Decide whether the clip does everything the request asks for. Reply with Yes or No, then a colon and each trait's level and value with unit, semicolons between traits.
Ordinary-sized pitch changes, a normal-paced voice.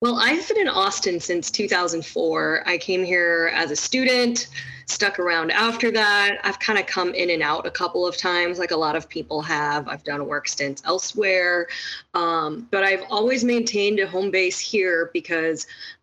Yes: average, 4.1 semitones; average, 185 wpm